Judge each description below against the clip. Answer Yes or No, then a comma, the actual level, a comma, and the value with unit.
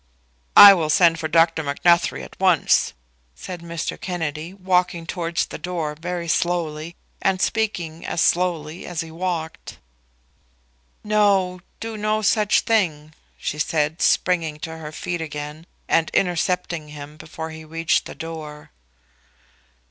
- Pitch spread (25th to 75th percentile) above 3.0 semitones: No, narrow, 2.4 semitones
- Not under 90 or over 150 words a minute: Yes, slow, 135 wpm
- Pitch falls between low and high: Yes, medium, 165 Hz